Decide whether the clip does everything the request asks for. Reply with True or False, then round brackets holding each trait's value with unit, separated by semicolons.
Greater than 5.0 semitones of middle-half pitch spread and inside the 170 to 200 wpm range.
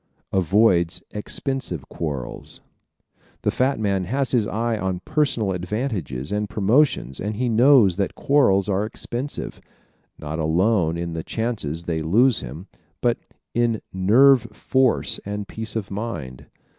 False (5.5 semitones; 135 wpm)